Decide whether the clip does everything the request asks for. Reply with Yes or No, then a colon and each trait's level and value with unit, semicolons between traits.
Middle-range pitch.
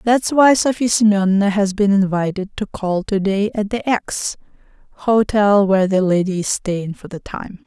No: high, 205 Hz